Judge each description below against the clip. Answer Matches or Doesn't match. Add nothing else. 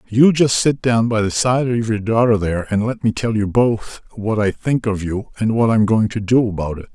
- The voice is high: Doesn't match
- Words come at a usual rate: Doesn't match